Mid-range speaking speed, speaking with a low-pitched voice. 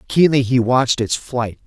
Yes: average, 180 wpm; low, 125 Hz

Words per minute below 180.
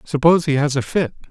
No: fast, 230 wpm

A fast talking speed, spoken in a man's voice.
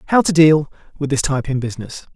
Yes: fast, 220 wpm; male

